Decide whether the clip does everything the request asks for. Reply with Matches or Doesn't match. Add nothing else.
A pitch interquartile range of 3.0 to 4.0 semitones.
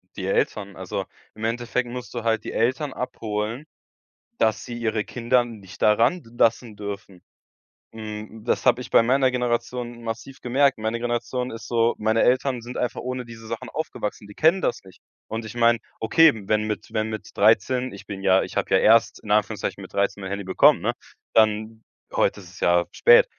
Doesn't match